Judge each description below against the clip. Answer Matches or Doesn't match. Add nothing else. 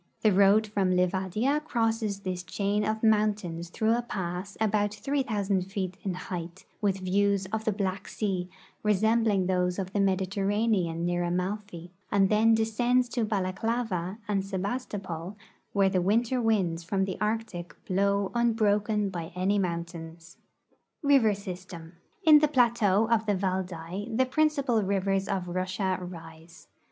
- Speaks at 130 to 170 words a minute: Matches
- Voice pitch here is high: Matches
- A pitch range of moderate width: Matches